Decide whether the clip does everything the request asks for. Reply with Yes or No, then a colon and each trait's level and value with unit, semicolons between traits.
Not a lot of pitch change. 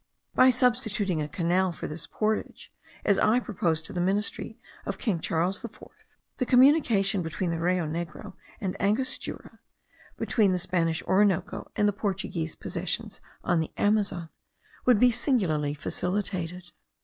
No: average, 4.1 semitones